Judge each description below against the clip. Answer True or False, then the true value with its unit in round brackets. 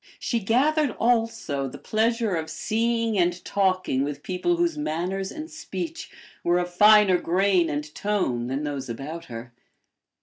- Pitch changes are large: True (6.7 semitones)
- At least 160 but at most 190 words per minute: False (145 wpm)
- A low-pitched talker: False (190 Hz)